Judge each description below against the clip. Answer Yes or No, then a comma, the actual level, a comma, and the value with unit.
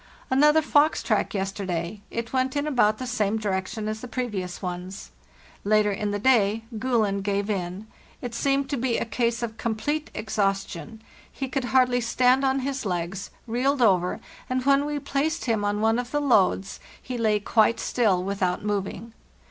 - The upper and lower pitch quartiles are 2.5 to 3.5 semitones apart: No, average, 4.4 semitones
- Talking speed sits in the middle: Yes, average, 170 wpm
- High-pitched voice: Yes, high, 225 Hz